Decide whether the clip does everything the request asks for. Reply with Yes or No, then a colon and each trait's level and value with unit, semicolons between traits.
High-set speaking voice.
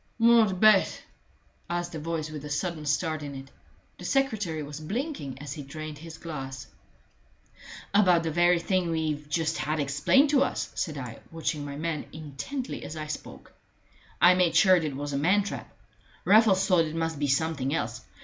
No: medium, 160 Hz